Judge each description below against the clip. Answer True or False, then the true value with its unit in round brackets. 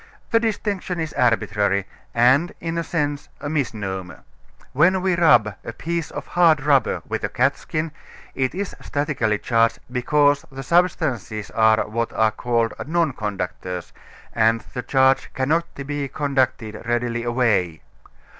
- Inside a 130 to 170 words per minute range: True (135 wpm)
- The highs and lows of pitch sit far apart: True (5.8 semitones)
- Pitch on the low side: True (130 Hz)